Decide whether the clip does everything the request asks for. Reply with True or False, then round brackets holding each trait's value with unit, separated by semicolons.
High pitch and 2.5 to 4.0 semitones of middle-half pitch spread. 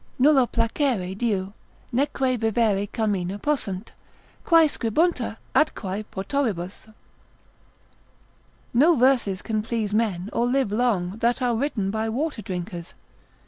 False (225 Hz; 4.6 semitones)